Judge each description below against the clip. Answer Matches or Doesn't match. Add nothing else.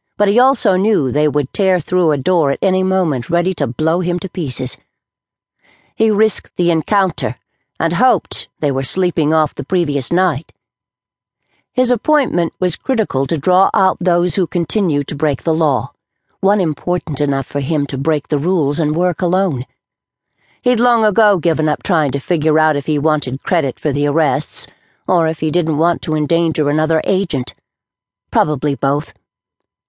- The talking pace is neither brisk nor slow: Matches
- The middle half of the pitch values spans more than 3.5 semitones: Matches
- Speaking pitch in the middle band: Matches